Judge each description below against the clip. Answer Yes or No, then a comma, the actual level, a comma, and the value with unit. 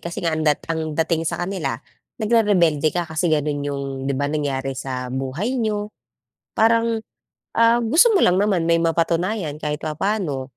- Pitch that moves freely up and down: Yes, wide, 6.0 semitones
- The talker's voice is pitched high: No, medium, 165 Hz